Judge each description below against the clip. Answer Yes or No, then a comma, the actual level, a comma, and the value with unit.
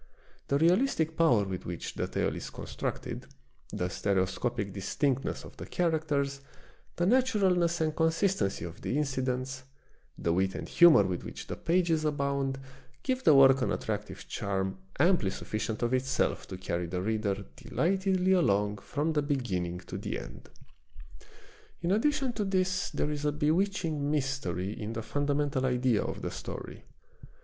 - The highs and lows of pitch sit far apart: Yes, wide, 8.4 semitones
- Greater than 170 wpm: No, average, 155 wpm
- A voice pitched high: No, medium, 140 Hz